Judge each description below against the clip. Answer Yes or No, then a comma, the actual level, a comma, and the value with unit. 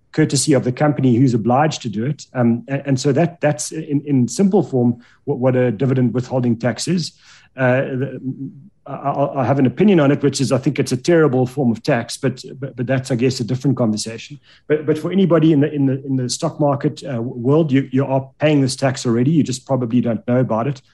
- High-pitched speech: No, low, 135 Hz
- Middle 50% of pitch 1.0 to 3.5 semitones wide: Yes, narrow, 2.6 semitones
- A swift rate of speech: Yes, fast, 225 wpm